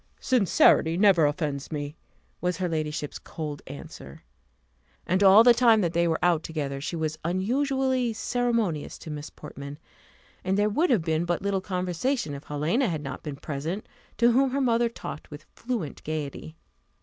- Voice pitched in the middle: Yes, medium, 175 Hz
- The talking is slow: No, average, 165 wpm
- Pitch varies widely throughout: Yes, wide, 7.0 semitones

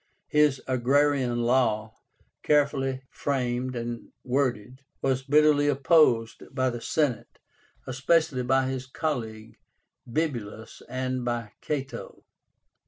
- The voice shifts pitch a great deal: No, average, 3.0 semitones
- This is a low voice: Yes, low, 130 Hz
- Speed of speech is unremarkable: No, slow, 100 wpm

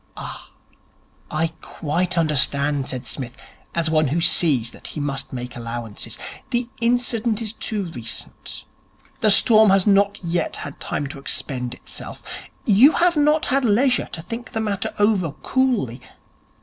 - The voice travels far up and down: Yes, wide, 8.1 semitones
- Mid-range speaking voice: Yes, medium, 175 Hz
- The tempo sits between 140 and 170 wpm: Yes, average, 150 wpm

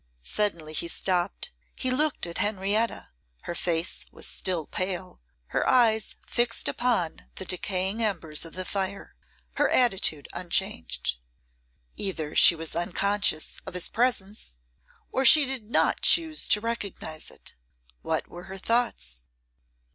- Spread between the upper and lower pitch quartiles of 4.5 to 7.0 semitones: Yes, average, 5.2 semitones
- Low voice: No, high, 190 Hz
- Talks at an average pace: No, slow, 130 wpm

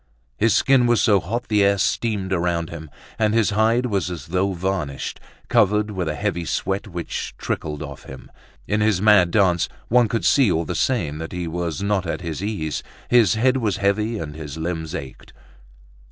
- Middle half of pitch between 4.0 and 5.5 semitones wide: Yes, average, 4.4 semitones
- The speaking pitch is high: No, very low, 95 Hz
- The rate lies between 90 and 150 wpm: No, average, 190 wpm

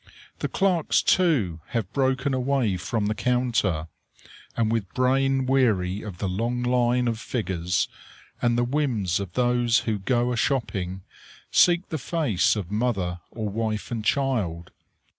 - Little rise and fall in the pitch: No, average, 4.6 semitones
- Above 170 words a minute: No, average, 145 wpm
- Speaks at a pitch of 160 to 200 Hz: No, low, 115 Hz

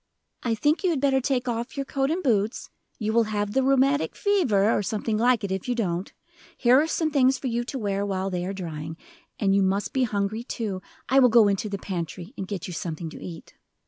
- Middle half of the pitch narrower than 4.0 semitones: No, average, 5.1 semitones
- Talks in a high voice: Yes, high, 220 Hz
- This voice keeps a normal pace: No, fast, 235 wpm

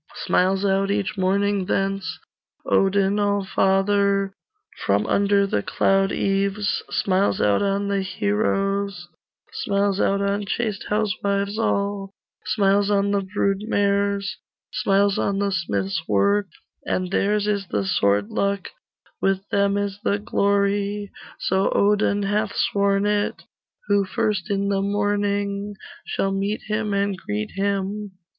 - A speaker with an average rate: No, slow, 125 wpm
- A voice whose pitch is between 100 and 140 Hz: No, high, 200 Hz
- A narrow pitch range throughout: Yes, narrow, 0.7 semitones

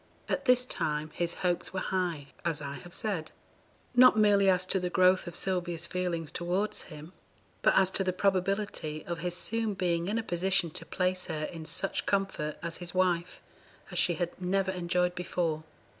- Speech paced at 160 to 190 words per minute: Yes, average, 185 wpm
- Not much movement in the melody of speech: Yes, narrow, 2.1 semitones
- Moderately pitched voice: Yes, medium, 180 Hz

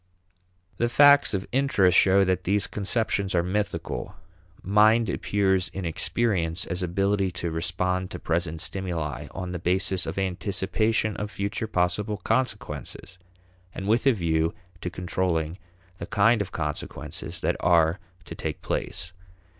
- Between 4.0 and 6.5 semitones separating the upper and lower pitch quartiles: No, average, 3.0 semitones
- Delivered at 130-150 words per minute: Yes, average, 140 wpm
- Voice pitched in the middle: No, very low, 95 Hz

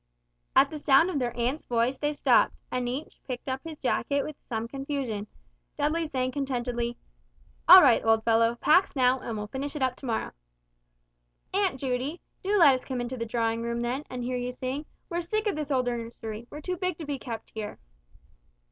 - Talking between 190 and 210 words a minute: Yes, average, 200 wpm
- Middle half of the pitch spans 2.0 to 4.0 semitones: Yes, average, 3.7 semitones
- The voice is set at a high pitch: Yes, very high, 255 Hz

